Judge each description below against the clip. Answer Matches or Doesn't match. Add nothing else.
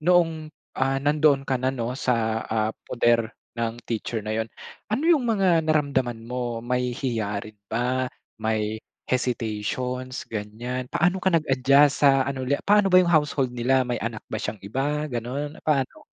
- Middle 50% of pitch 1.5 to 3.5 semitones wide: Doesn't match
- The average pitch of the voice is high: Doesn't match